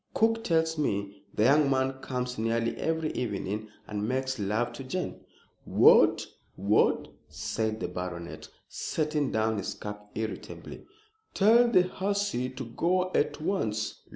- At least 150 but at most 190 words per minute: No, slow, 135 wpm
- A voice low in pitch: Yes, low, 125 Hz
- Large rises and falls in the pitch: Yes, wide, 7.0 semitones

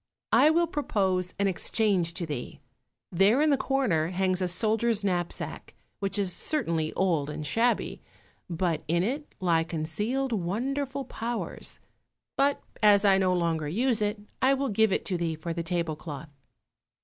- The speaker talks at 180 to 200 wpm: No, average, 160 wpm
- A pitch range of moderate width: No, wide, 5.8 semitones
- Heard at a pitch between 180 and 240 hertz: Yes, high, 190 Hz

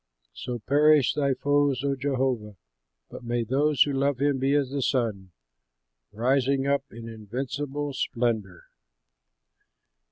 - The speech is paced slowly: Yes, slow, 125 wpm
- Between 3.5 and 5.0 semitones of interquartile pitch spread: No, average, 3.0 semitones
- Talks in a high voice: No, low, 135 Hz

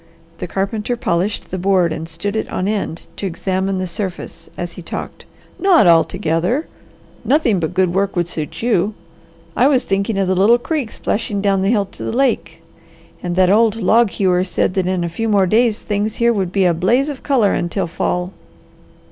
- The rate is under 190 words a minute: No, average, 195 wpm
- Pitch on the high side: Yes, high, 195 Hz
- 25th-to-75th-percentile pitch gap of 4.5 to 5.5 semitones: No, average, 3.7 semitones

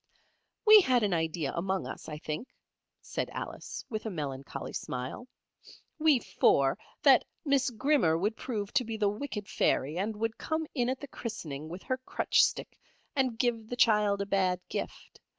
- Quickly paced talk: No, average, 170 wpm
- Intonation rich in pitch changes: Yes, wide, 6.8 semitones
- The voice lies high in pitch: Yes, high, 210 Hz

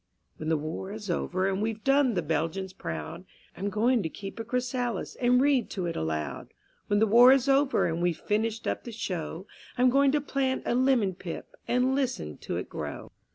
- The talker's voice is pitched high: Yes, high, 215 Hz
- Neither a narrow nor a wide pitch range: No, wide, 6.1 semitones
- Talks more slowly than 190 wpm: No, average, 200 wpm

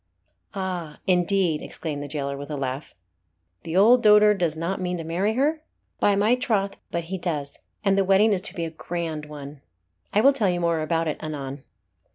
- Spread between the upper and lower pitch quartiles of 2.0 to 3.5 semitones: No, average, 4.4 semitones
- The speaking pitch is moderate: Yes, medium, 175 Hz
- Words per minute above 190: Yes, average, 200 wpm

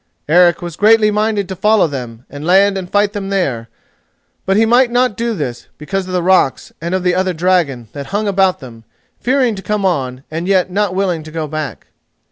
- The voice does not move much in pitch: No, average, 4.7 semitones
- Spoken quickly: Yes, fast, 210 wpm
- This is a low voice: No, medium, 185 Hz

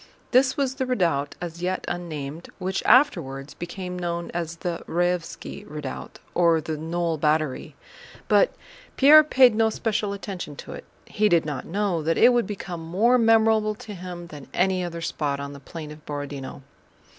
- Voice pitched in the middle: Yes, medium, 175 Hz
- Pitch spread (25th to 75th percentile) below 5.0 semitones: No, average, 5.3 semitones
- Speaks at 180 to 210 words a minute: No, average, 170 wpm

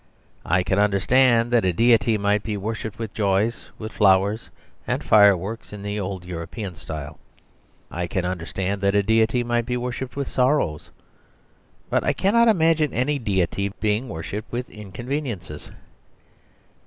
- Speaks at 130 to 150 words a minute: Yes, average, 145 wpm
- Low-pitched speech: Yes, low, 105 Hz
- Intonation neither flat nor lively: Yes, average, 4.0 semitones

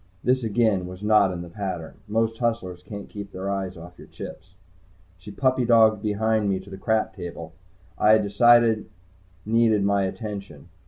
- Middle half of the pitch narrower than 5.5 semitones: Yes, average, 2.9 semitones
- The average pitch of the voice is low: Yes, low, 105 Hz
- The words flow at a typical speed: Yes, average, 170 wpm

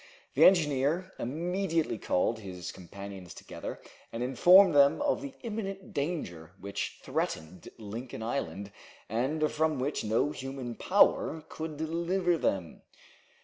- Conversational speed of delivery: No, slow, 120 wpm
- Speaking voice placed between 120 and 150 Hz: Yes, medium, 140 Hz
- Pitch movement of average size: No, wide, 8.3 semitones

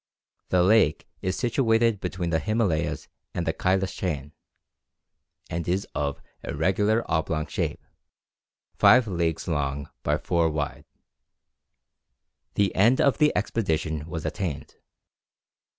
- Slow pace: Yes, slow, 115 wpm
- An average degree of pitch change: Yes, average, 4.8 semitones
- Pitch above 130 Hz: No, very low, 90 Hz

